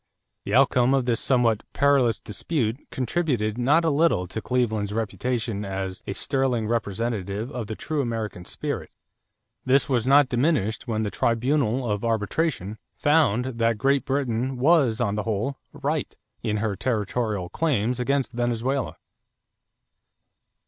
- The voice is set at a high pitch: No, low, 120 Hz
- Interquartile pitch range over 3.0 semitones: Yes, average, 3.9 semitones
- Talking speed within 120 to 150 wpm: Yes, slow, 135 wpm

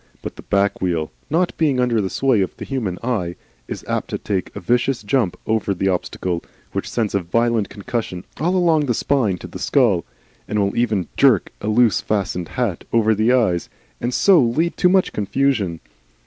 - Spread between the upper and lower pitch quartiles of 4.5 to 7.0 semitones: Yes, average, 5.0 semitones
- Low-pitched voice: Yes, low, 110 Hz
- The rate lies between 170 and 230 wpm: Yes, average, 190 wpm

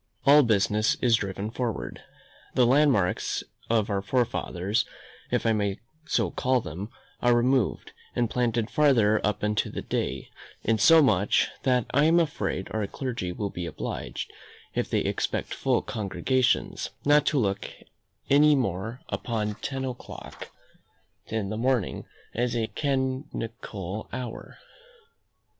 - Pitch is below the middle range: Yes, low, 115 Hz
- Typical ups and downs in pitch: Yes, average, 4.0 semitones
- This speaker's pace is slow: Yes, slow, 130 wpm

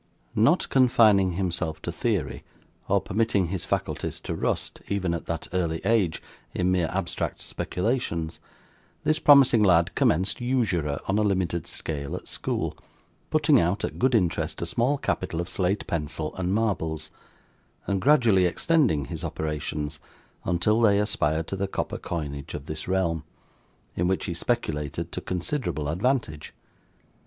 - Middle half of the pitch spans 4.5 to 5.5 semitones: Yes, average, 5.1 semitones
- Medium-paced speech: Yes, average, 145 wpm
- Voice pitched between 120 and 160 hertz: No, very low, 90 Hz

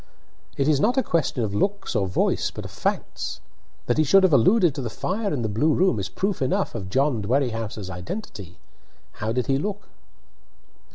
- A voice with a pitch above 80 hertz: Yes, low, 135 Hz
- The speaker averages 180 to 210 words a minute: Yes, average, 190 wpm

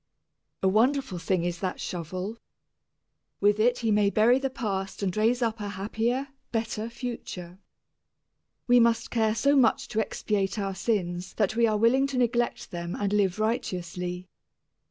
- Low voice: No, high, 215 Hz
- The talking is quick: No, average, 155 wpm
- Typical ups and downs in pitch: Yes, average, 3.8 semitones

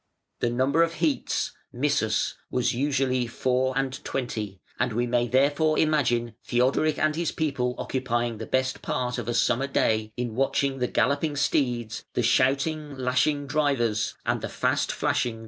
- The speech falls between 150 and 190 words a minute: Yes, average, 165 wpm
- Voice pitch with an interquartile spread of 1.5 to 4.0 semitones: Yes, average, 3.0 semitones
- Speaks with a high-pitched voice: No, low, 130 Hz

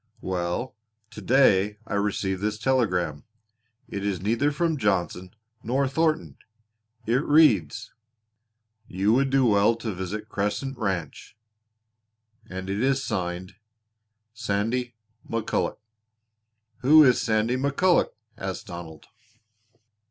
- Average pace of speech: No, slow, 105 wpm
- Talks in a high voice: No, low, 110 Hz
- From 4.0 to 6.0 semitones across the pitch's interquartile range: Yes, wide, 5.5 semitones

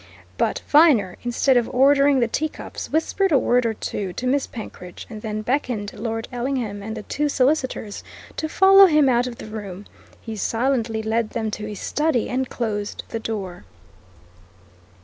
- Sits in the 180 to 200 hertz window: No, high, 235 Hz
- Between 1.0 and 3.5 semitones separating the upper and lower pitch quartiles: No, average, 4.3 semitones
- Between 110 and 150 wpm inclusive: No, average, 170 wpm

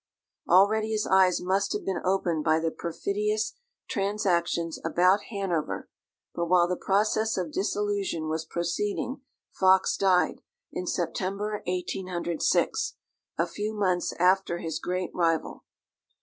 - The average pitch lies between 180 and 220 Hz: Yes, medium, 185 Hz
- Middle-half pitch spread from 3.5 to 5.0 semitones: No, average, 2.8 semitones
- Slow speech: Yes, slow, 120 wpm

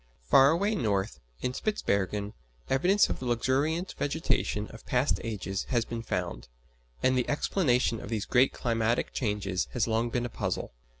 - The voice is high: No, low, 120 Hz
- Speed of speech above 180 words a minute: No, average, 160 wpm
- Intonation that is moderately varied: Yes, average, 4.1 semitones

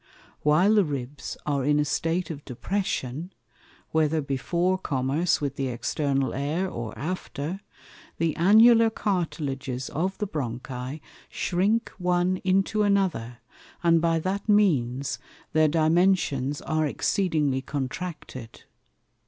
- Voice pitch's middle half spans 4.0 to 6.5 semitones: Yes, average, 5.2 semitones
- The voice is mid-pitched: Yes, medium, 155 Hz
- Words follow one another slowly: Yes, slow, 115 wpm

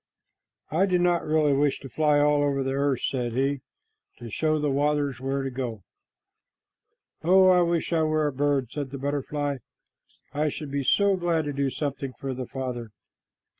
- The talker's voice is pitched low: No, medium, 145 Hz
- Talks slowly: No, average, 180 wpm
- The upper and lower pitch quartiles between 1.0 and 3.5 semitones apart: Yes, narrow, 2.5 semitones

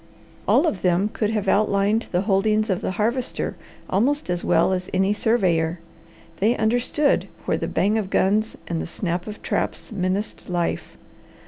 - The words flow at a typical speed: Yes, average, 160 wpm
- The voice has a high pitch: Yes, high, 200 Hz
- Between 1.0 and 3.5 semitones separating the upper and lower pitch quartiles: Yes, average, 3.0 semitones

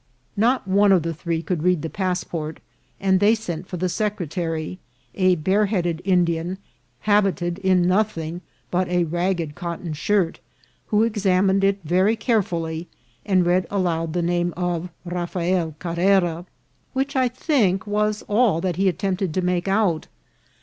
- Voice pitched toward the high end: No, medium, 180 Hz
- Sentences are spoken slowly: No, average, 150 wpm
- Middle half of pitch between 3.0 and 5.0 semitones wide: No, narrow, 2.6 semitones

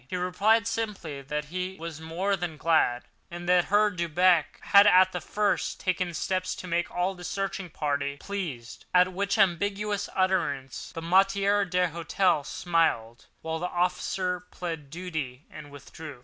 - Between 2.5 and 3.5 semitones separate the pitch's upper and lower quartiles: Yes, average, 3.2 semitones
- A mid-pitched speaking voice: Yes, medium, 180 Hz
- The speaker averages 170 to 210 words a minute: No, average, 150 wpm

